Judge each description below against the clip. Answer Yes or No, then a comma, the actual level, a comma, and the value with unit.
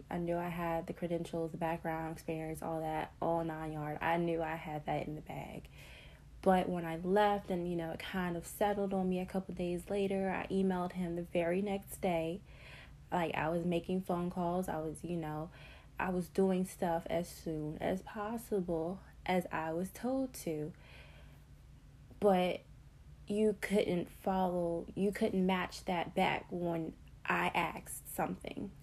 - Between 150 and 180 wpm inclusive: Yes, average, 175 wpm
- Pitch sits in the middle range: Yes, medium, 175 Hz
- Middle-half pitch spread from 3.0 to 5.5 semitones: No, narrow, 2.5 semitones